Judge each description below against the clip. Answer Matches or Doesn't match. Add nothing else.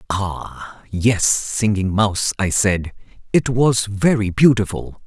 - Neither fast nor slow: Doesn't match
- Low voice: Matches